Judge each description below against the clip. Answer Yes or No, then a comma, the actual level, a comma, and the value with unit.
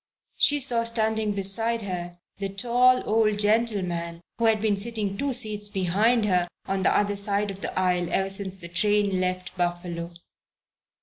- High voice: Yes, high, 200 Hz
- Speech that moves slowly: No, average, 160 wpm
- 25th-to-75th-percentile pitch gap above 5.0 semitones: No, average, 3.2 semitones